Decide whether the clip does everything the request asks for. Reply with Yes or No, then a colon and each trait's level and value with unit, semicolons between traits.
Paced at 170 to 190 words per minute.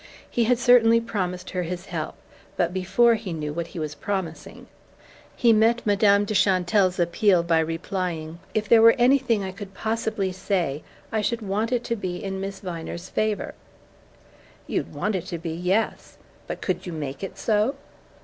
Yes: average, 175 wpm